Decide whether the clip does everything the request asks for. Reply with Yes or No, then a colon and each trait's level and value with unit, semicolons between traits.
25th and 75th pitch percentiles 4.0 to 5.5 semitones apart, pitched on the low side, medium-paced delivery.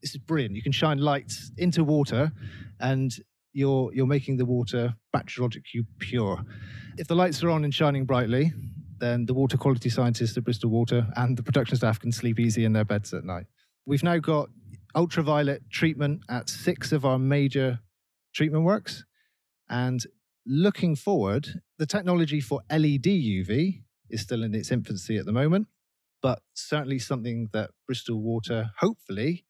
Yes: average, 4.6 semitones; low, 130 Hz; average, 165 wpm